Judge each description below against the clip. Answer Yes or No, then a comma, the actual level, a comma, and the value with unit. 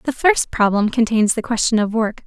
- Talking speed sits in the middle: No, fast, 210 wpm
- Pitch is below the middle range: No, high, 225 Hz